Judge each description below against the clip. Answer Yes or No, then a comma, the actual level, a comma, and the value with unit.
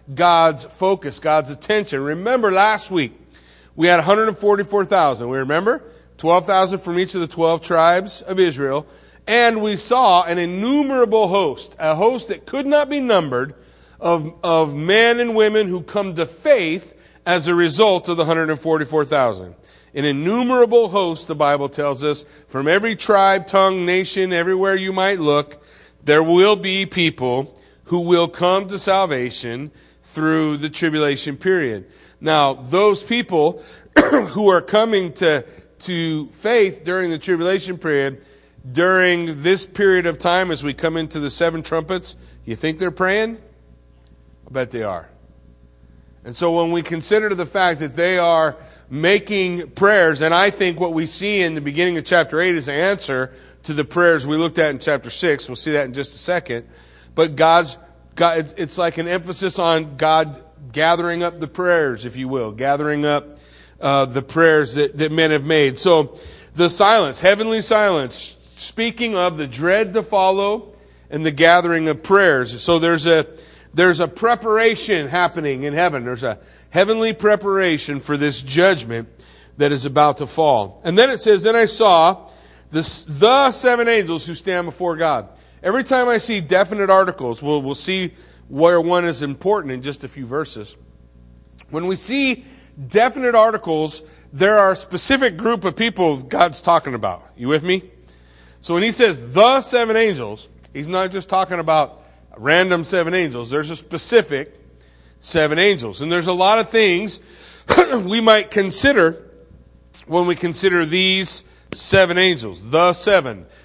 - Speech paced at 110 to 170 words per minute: Yes, average, 160 wpm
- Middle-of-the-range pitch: Yes, medium, 170 Hz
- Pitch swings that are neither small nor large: Yes, average, 4.8 semitones